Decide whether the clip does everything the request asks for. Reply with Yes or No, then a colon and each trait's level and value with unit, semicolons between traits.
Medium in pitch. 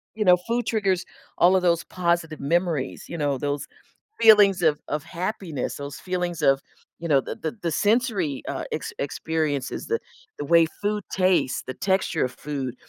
Yes: medium, 170 Hz